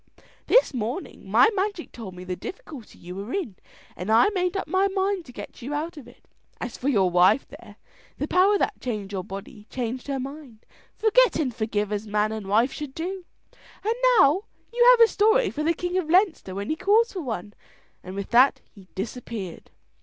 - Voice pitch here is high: Yes, very high, 265 Hz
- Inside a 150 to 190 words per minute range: No, average, 200 wpm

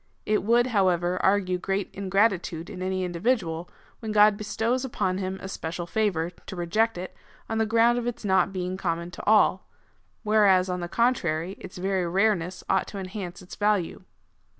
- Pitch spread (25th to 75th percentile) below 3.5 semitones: Yes, average, 3.1 semitones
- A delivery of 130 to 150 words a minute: No, average, 175 wpm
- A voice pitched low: No, high, 190 Hz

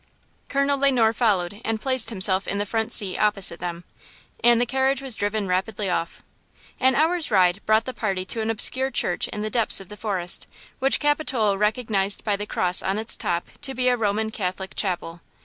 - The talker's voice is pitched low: No, high, 215 Hz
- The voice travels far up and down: No, average, 4.4 semitones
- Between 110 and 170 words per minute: No, average, 200 wpm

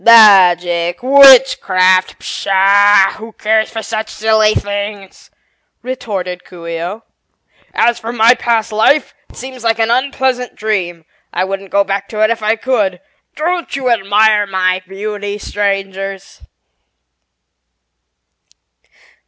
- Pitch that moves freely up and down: No, average, 2.9 semitones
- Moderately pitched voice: No, high, 210 Hz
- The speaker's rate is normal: No, slow, 120 wpm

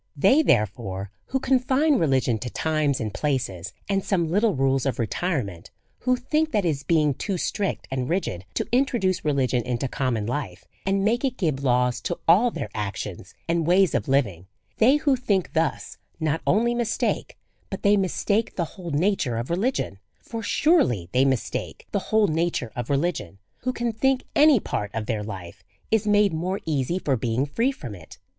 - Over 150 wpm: Yes, average, 180 wpm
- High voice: No, medium, 160 Hz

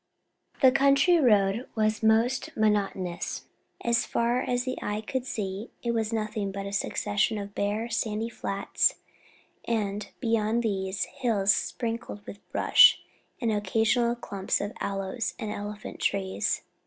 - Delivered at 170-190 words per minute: No, slow, 135 wpm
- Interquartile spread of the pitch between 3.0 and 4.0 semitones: No, narrow, 2.6 semitones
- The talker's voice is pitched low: No, high, 215 Hz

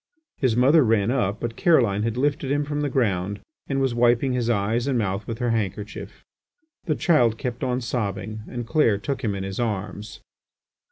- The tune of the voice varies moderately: Yes, average, 4.0 semitones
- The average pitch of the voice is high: No, low, 120 Hz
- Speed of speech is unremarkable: Yes, average, 185 wpm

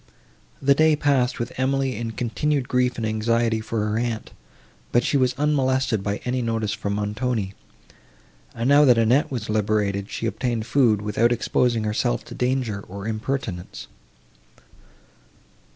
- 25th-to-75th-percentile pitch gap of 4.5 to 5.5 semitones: No, average, 3.2 semitones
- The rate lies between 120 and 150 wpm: Yes, average, 145 wpm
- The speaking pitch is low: Yes, low, 115 Hz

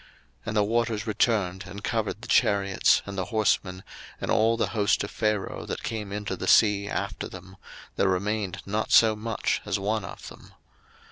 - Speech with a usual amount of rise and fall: No, narrow, 1.9 semitones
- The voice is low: Yes, low, 105 Hz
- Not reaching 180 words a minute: No, average, 185 wpm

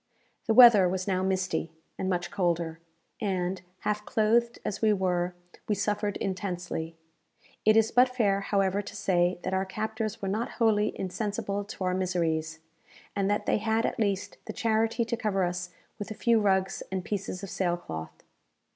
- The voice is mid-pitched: No, high, 195 Hz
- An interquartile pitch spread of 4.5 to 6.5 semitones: No, average, 2.8 semitones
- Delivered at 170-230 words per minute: Yes, average, 175 wpm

